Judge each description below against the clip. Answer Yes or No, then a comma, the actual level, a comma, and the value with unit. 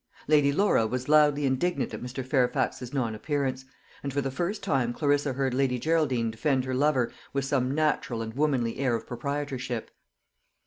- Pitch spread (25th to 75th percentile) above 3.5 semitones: No, narrow, 2.6 semitones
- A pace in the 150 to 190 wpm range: Yes, average, 170 wpm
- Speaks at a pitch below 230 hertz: Yes, low, 135 Hz